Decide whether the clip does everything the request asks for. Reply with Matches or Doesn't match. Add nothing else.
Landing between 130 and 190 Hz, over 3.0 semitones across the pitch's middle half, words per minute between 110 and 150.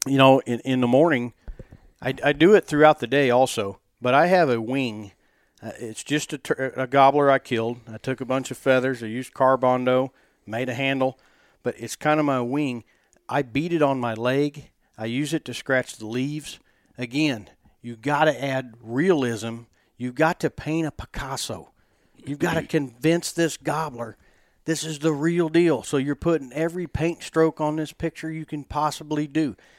Doesn't match